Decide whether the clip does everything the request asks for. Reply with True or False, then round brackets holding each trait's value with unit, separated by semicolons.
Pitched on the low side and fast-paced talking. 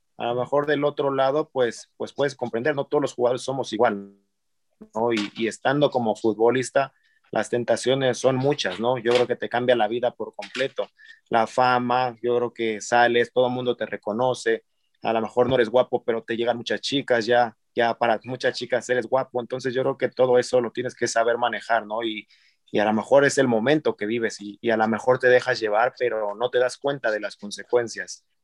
True (120 Hz; 215 wpm)